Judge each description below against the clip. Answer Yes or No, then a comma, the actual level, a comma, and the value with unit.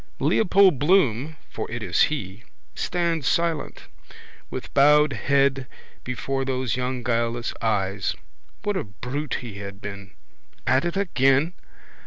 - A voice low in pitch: Yes, low, 130 Hz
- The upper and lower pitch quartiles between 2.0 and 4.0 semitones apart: No, average, 4.9 semitones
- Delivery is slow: Yes, slow, 125 wpm